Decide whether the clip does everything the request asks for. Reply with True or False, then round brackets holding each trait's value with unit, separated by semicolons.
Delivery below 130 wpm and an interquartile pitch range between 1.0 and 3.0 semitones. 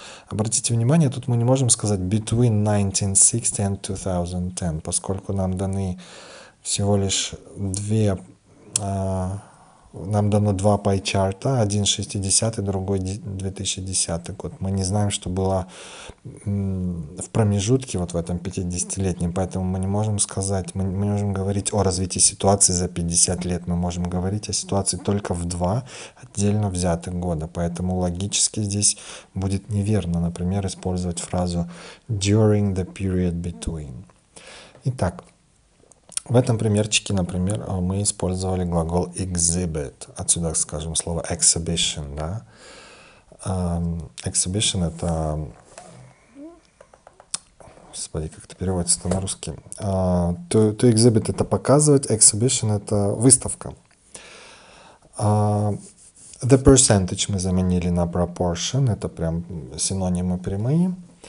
True (115 wpm; 2.7 semitones)